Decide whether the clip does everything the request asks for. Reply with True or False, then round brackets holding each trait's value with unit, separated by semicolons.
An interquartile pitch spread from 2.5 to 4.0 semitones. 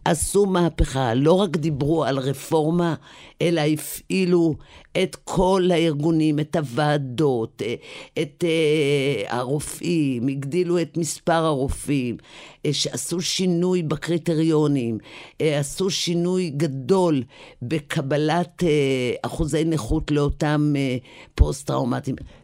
True (3.1 semitones)